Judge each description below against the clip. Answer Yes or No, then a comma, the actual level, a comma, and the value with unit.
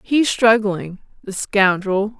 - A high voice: Yes, high, 205 Hz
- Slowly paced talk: Yes, slow, 110 wpm